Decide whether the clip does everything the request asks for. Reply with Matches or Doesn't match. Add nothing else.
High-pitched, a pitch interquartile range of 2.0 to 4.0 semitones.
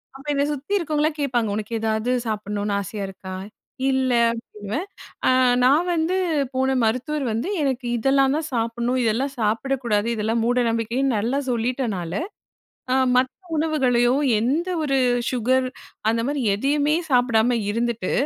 Matches